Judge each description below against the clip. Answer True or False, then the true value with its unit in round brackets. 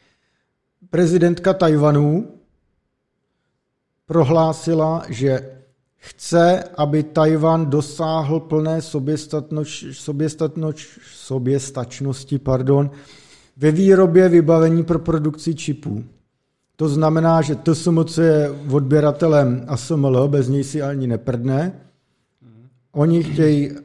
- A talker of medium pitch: True (150 Hz)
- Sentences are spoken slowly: True (90 wpm)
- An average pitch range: True (3.0 semitones)